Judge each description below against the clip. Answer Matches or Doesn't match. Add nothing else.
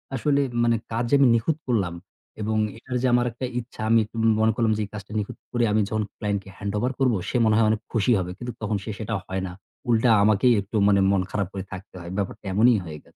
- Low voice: Matches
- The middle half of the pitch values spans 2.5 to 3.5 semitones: Matches